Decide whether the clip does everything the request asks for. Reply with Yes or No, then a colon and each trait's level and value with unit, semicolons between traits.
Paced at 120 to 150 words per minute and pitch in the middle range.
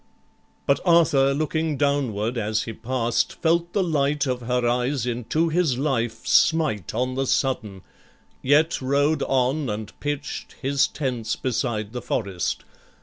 No: average, 140 wpm; low, 130 Hz